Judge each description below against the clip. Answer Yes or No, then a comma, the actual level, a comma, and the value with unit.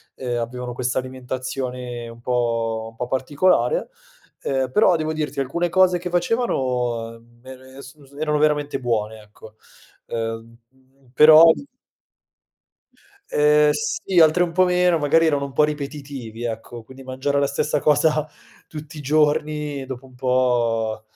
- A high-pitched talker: No, low, 135 Hz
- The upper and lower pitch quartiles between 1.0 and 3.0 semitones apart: No, average, 3.8 semitones